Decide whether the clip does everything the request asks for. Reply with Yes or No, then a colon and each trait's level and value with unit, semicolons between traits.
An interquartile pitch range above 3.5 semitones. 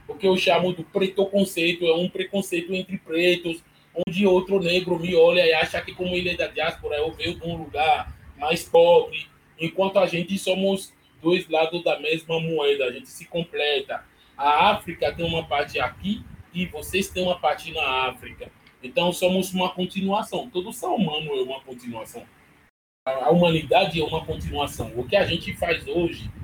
No: average, 3.0 semitones